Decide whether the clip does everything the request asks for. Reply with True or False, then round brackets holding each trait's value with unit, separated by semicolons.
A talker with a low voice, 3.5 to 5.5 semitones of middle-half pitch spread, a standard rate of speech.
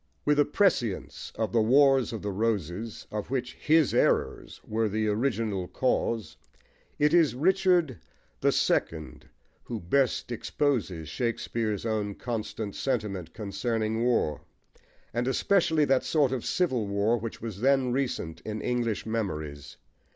False (115 Hz; 4.2 semitones; 130 wpm)